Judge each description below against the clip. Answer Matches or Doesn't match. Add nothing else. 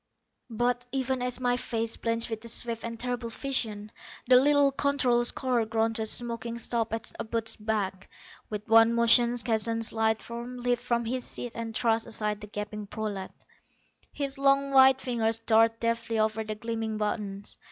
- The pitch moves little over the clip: Matches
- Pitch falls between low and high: Doesn't match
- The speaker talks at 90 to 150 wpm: Doesn't match